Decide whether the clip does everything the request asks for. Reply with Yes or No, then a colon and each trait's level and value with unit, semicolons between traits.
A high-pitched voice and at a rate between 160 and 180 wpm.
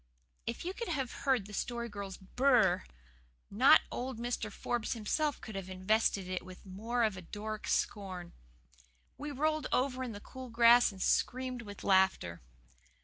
Yes: high, 225 Hz; average, 175 wpm